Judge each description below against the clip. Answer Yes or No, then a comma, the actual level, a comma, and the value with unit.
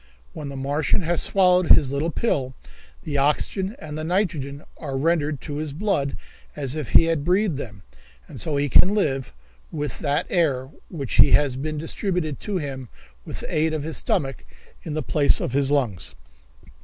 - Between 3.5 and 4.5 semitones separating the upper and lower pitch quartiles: No, average, 3.1 semitones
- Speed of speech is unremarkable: Yes, average, 180 wpm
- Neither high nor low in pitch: Yes, medium, 150 Hz